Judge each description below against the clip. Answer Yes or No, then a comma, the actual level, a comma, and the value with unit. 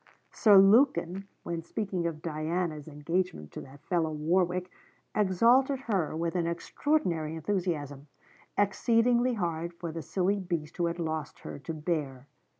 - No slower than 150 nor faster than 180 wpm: No, average, 140 wpm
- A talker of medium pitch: Yes, medium, 170 Hz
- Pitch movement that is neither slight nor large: Yes, average, 3.6 semitones